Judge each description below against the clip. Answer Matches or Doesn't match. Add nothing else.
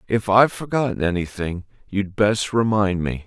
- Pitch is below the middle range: Matches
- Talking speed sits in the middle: Matches